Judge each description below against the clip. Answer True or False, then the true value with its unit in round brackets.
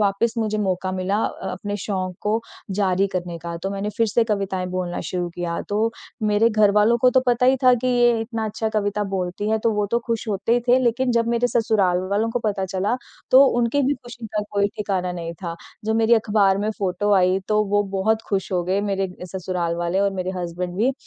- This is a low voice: False (205 Hz)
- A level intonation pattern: False (3.3 semitones)